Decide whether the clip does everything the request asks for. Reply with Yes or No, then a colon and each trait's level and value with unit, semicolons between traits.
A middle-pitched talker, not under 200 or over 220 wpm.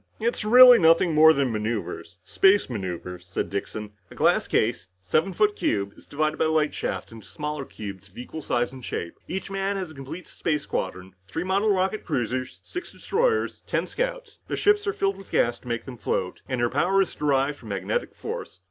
Yes: medium, 150 Hz; fast, 205 wpm